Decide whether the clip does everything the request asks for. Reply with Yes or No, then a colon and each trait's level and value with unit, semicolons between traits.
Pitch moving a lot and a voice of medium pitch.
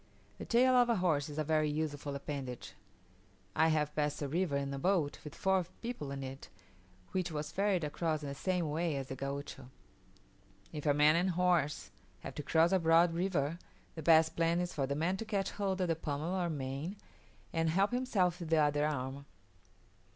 No: average, 3.8 semitones; medium, 160 Hz